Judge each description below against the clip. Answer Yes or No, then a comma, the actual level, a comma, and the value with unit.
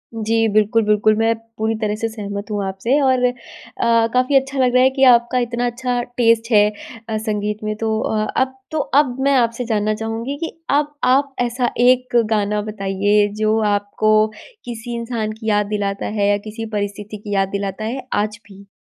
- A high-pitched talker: Yes, high, 220 Hz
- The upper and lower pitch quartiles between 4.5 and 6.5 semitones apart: No, average, 2.8 semitones